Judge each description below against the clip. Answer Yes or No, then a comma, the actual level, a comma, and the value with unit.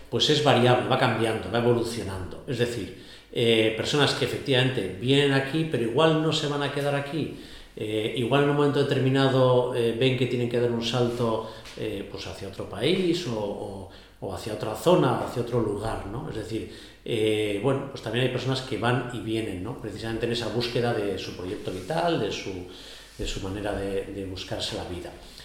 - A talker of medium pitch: No, low, 115 Hz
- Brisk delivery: Yes, fast, 200 wpm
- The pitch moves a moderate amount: Yes, average, 4.0 semitones